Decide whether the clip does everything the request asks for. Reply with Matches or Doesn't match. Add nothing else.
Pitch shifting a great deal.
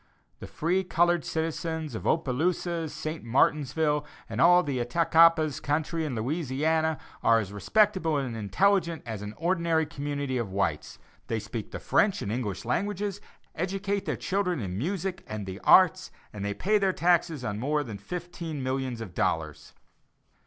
Matches